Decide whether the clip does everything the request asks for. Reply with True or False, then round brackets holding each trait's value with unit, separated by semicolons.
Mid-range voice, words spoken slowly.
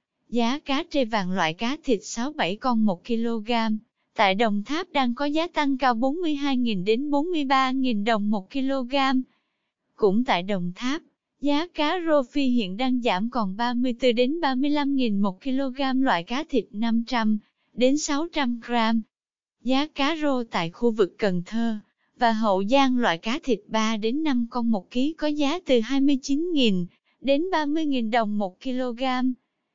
False (250 Hz; 155 wpm)